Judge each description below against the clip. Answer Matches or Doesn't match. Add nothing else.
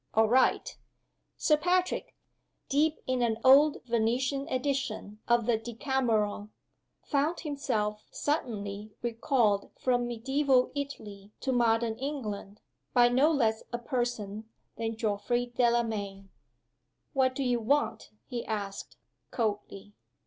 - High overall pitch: Matches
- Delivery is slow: Matches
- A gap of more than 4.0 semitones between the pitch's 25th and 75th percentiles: Doesn't match